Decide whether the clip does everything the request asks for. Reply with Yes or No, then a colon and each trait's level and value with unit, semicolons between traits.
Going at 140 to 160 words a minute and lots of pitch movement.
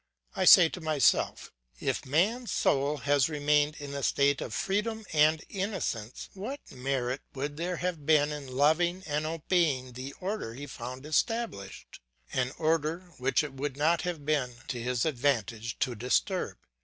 No: average, 155 wpm; average, 4.2 semitones